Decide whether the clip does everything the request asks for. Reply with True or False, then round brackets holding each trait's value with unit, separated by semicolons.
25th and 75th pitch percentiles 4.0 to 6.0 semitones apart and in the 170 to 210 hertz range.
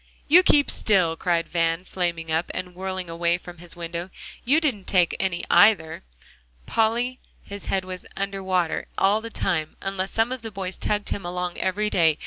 False (3.2 semitones; 185 Hz)